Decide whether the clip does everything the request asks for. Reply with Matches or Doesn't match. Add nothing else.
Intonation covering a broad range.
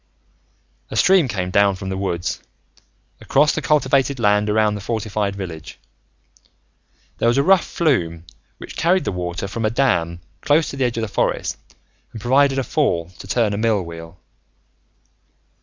Matches